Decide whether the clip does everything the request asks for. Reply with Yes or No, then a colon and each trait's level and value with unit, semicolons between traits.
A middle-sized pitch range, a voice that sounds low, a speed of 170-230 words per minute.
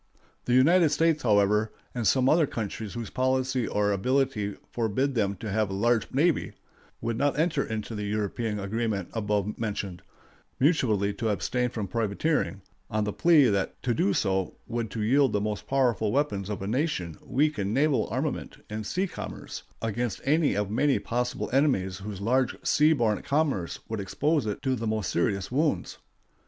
Yes: average, 4.7 semitones; low, 115 Hz; average, 175 wpm